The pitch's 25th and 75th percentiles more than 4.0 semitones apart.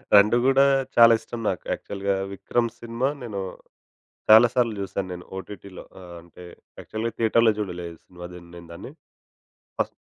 Yes: average, 4.5 semitones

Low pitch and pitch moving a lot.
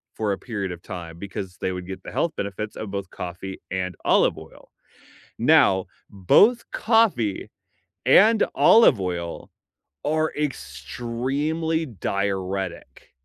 Yes: low, 100 Hz; wide, 8.0 semitones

